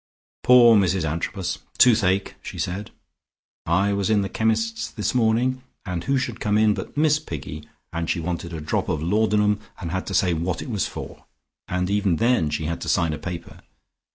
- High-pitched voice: No, low, 100 Hz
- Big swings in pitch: No, average, 4.6 semitones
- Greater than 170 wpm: Yes, average, 190 wpm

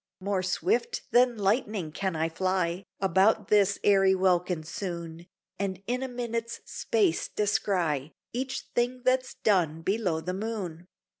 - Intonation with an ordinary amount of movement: Yes, average, 4.8 semitones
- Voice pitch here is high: Yes, high, 195 Hz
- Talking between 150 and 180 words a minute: No, slow, 135 wpm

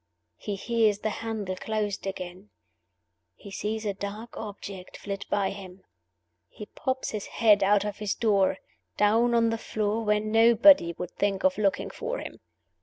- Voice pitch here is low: No, high, 210 Hz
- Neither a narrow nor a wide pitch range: No, narrow, 2.2 semitones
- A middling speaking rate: Yes, average, 160 wpm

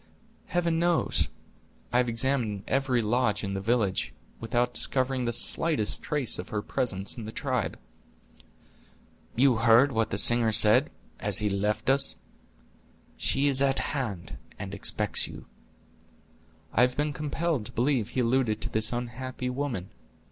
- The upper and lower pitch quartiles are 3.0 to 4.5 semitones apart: Yes, average, 4.0 semitones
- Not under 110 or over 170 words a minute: Yes, average, 150 wpm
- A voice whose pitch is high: No, low, 120 Hz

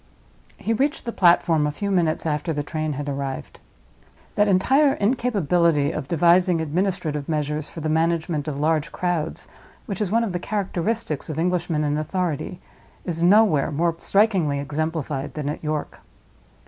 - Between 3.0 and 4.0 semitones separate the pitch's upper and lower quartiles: Yes, average, 3.7 semitones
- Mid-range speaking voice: Yes, medium, 165 Hz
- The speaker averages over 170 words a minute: No, average, 155 wpm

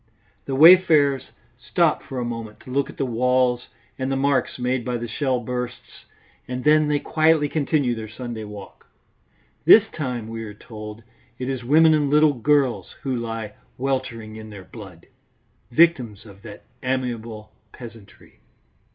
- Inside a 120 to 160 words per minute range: Yes, average, 155 wpm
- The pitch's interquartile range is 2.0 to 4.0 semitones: Yes, average, 3.7 semitones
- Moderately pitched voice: No, low, 125 Hz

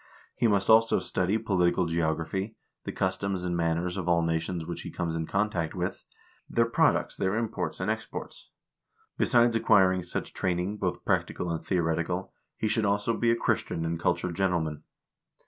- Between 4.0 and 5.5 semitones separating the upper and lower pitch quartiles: No, average, 3.3 semitones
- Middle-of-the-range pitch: No, very low, 90 Hz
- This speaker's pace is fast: No, average, 165 wpm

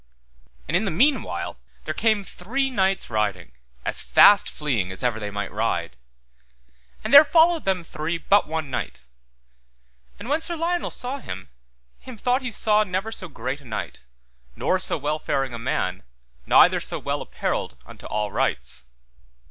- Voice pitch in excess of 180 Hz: No, medium, 165 Hz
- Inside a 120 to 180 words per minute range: Yes, average, 165 wpm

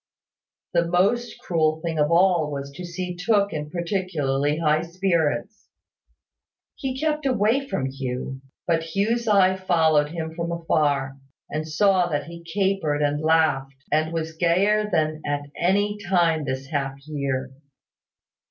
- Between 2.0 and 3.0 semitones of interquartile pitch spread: No, average, 4.2 semitones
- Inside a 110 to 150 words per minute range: Yes, average, 140 wpm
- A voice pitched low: No, medium, 165 Hz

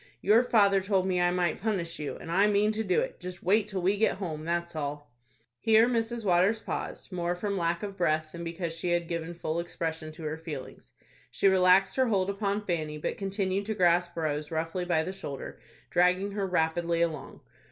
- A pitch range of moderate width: Yes, average, 3.1 semitones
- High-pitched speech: No, medium, 180 Hz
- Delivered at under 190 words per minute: No, fast, 205 wpm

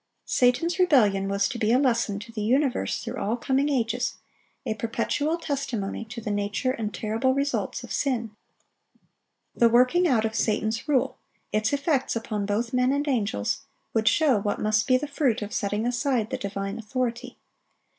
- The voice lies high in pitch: Yes, high, 235 Hz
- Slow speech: No, average, 170 wpm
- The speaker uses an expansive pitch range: No, average, 3.8 semitones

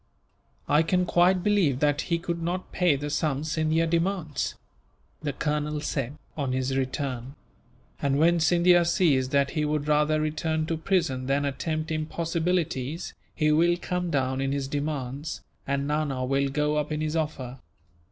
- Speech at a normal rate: Yes, average, 160 wpm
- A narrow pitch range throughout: No, average, 3.1 semitones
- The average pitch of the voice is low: No, medium, 150 Hz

